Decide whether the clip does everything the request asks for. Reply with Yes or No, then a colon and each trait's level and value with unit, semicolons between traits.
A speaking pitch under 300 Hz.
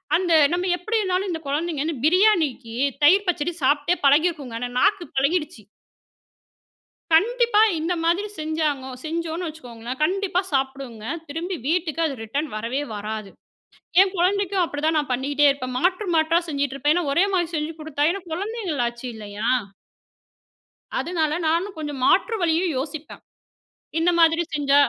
No: very high, 315 Hz